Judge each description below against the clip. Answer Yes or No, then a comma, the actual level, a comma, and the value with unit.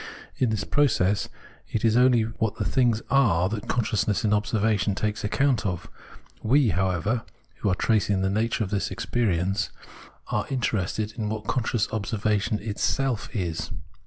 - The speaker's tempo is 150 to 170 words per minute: Yes, average, 155 wpm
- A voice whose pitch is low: Yes, low, 110 Hz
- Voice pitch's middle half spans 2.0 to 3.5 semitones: Yes, narrow, 2.6 semitones